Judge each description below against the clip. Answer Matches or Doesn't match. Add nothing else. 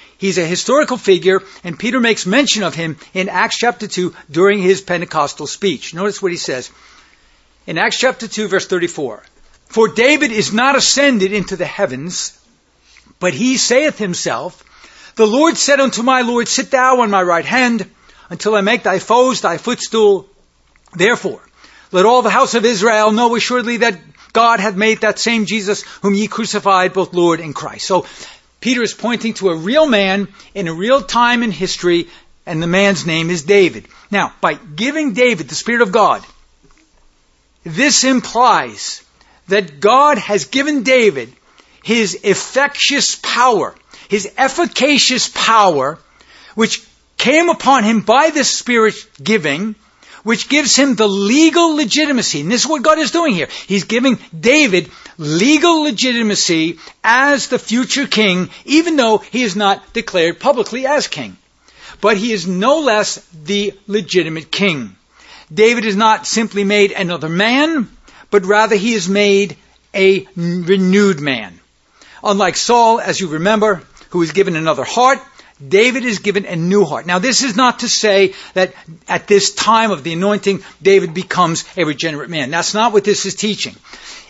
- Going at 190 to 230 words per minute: Doesn't match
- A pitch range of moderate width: Matches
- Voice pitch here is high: Matches